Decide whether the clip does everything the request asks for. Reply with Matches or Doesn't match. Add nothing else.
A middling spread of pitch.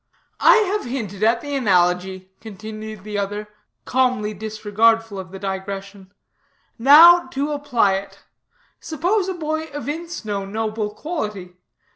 Doesn't match